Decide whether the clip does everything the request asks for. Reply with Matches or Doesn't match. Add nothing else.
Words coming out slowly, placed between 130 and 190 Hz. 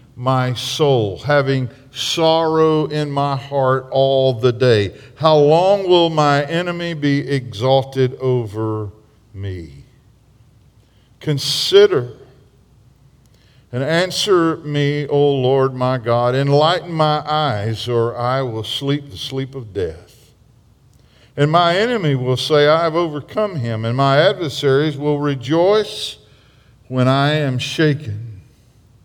Matches